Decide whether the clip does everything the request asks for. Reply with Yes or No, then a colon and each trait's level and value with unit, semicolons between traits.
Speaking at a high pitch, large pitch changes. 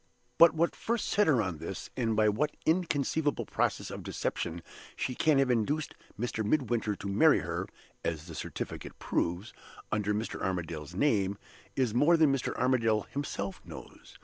No: low, 115 Hz; wide, 6.7 semitones